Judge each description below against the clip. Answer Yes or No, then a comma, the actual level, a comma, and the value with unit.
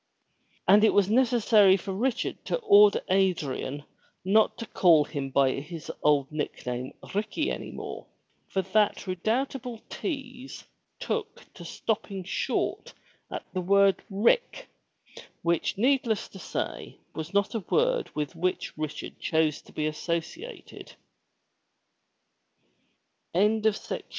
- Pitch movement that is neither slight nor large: No, wide, 6.0 semitones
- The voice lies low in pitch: No, high, 195 Hz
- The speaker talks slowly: Yes, slow, 110 wpm